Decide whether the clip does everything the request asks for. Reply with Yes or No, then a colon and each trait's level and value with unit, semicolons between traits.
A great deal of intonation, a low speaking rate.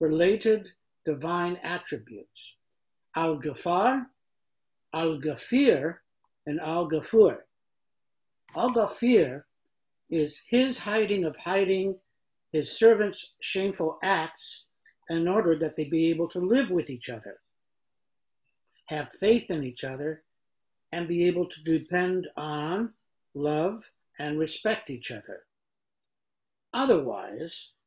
No: average, 4.9 semitones; slow, 105 wpm